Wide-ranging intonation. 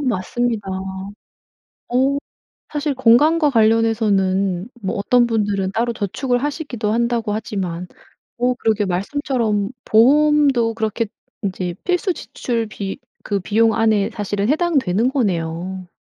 No: average, 4.0 semitones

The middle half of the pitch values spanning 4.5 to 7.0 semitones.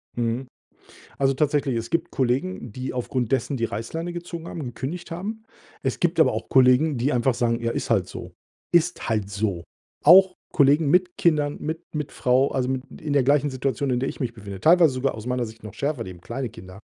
Yes: average, 4.9 semitones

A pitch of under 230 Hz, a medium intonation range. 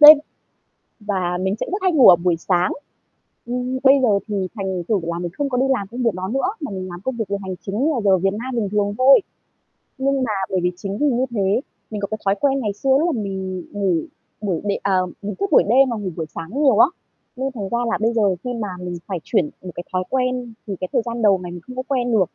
Yes: high, 210 Hz; average, 4.9 semitones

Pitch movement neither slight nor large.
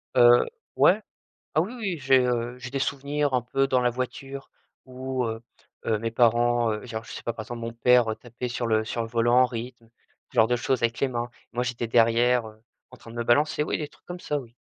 No: narrow, 2.1 semitones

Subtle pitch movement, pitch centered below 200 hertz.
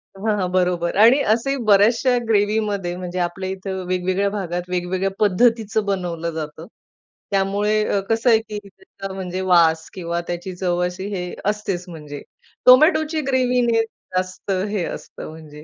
No: average, 3.4 semitones; high, 190 Hz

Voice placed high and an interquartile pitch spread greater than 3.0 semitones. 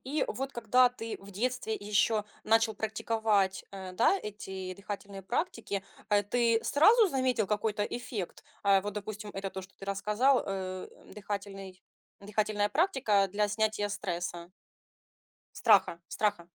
No: high, 210 Hz; narrow, 2.5 semitones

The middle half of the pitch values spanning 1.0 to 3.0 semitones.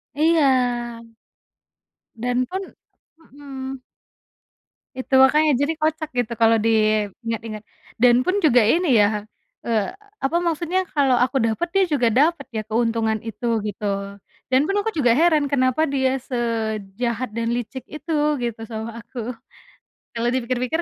No: average, 4.1 semitones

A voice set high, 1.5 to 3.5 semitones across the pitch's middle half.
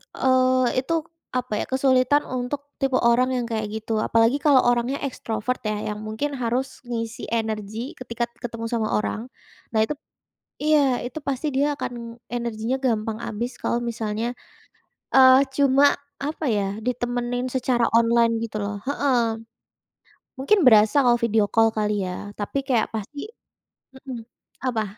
Yes: high, 240 Hz; average, 2.8 semitones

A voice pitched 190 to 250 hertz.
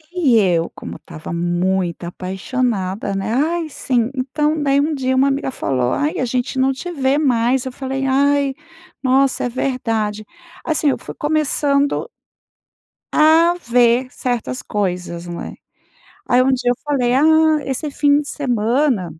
No: very high, 260 Hz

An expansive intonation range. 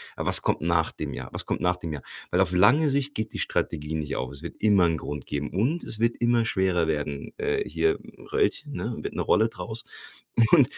Yes: wide, 7.1 semitones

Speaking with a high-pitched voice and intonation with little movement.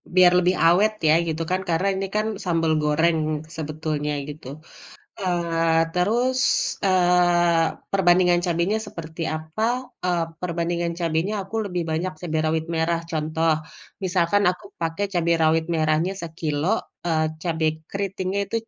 No: medium, 170 Hz; narrow, 2.2 semitones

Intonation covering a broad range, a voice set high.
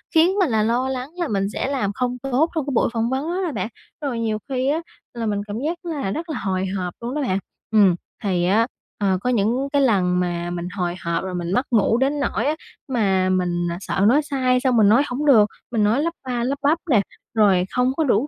Yes: wide, 5.9 semitones; high, 235 Hz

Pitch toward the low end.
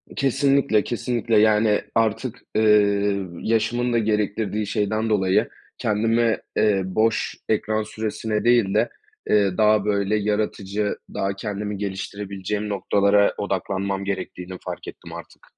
Yes: low, 105 Hz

